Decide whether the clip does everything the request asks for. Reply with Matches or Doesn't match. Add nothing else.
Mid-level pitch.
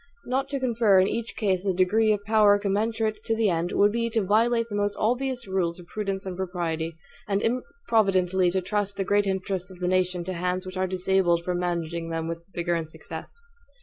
Doesn't match